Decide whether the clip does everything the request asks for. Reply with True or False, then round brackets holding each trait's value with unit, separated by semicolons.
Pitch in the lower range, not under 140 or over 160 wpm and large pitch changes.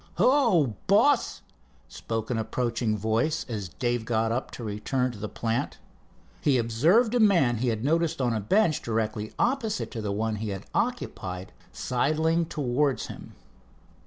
True (120 Hz; 155 wpm; 6.7 semitones)